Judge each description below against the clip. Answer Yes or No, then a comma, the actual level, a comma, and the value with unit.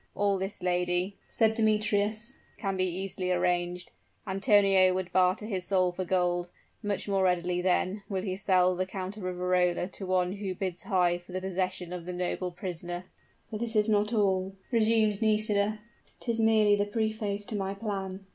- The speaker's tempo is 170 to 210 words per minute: Yes, average, 175 wpm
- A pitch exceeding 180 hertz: Yes, high, 190 Hz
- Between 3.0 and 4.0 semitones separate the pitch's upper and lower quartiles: No, narrow, 2.4 semitones